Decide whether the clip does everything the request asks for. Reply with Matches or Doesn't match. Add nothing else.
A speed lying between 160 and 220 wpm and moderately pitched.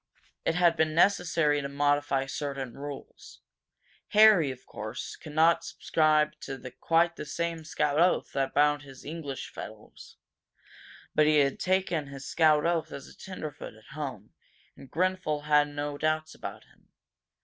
Doesn't match